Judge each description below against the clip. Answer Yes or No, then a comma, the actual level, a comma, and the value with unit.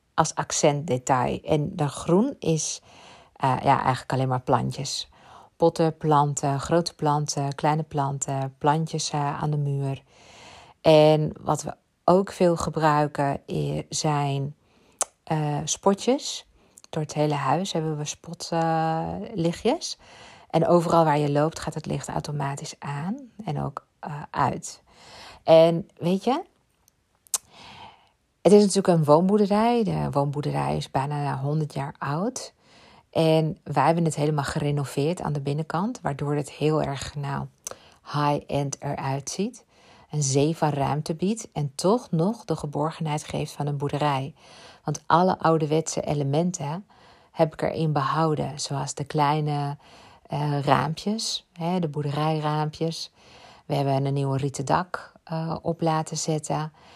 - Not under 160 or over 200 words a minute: No, slow, 135 wpm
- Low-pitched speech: No, medium, 150 Hz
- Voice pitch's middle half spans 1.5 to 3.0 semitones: Yes, narrow, 2.4 semitones